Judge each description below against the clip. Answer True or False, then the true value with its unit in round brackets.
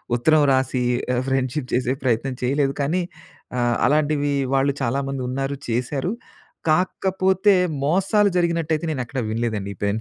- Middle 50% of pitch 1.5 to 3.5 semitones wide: False (3.9 semitones)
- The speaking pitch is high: False (135 Hz)